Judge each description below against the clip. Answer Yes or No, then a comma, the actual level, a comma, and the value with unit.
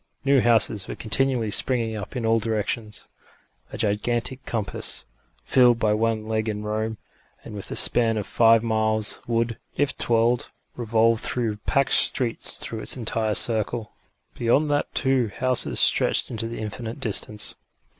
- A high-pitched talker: No, low, 115 Hz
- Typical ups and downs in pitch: No, narrow, 1.7 semitones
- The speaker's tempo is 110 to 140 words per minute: No, average, 150 wpm